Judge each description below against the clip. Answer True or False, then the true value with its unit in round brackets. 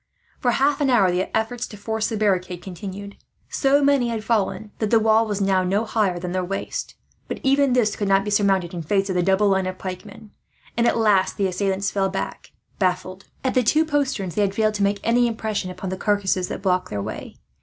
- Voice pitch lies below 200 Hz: False (205 Hz)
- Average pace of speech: False (225 wpm)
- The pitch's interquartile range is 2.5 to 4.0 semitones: True (3.0 semitones)